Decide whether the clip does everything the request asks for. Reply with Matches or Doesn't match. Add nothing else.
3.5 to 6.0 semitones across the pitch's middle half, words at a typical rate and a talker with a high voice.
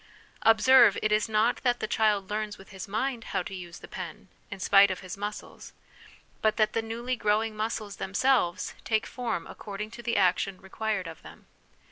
Doesn't match